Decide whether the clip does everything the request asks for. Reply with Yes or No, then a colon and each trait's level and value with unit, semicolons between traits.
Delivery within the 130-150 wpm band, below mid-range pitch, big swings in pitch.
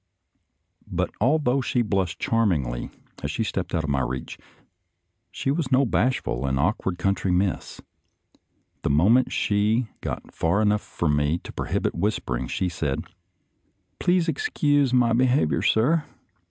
Yes: average, 140 wpm; low, 105 Hz; wide, 8.2 semitones